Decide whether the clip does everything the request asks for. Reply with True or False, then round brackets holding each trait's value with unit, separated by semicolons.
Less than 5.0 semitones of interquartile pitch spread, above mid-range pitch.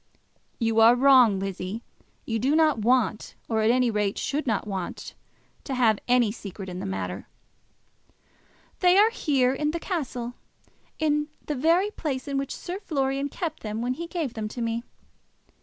False (5.4 semitones; 250 Hz)